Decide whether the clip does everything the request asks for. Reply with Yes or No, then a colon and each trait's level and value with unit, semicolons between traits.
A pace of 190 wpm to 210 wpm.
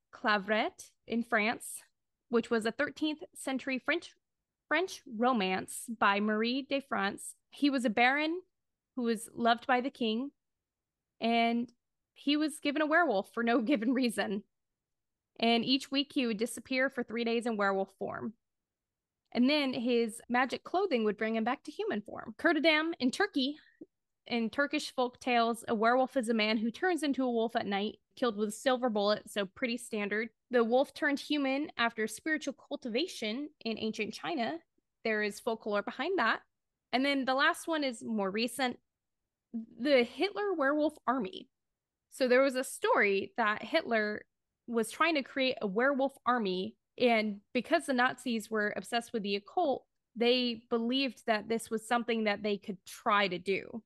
No: average, 165 wpm